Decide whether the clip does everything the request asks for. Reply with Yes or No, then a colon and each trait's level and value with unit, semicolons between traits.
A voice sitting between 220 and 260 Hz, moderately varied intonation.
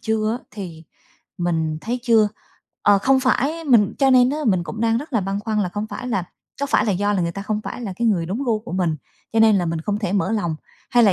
No: high, 210 Hz; average, 4.1 semitones